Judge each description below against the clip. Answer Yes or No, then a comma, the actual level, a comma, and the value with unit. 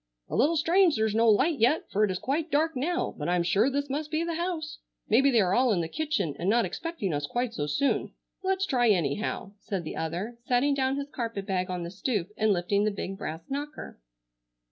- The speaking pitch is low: No, high, 235 Hz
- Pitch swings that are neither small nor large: No, wide, 7.2 semitones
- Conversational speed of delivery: No, fast, 225 wpm